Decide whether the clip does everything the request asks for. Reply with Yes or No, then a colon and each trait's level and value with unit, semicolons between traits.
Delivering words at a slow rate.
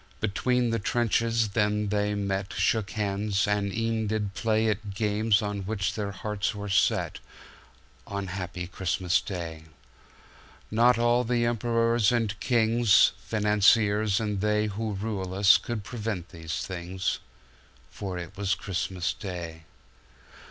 Yes: slow, 115 wpm